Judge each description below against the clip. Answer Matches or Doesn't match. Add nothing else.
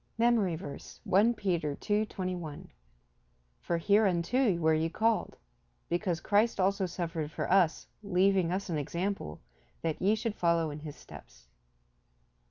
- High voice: Doesn't match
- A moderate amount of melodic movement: Matches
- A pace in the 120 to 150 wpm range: Matches